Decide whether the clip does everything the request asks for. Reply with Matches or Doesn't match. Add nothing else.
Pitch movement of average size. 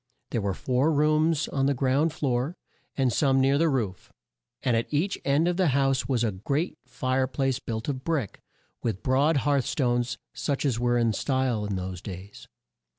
Matches